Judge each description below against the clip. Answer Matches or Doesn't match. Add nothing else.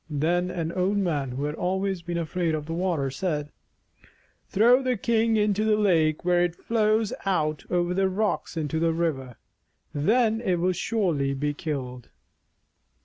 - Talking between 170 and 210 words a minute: Doesn't match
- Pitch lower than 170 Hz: Doesn't match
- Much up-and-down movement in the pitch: Doesn't match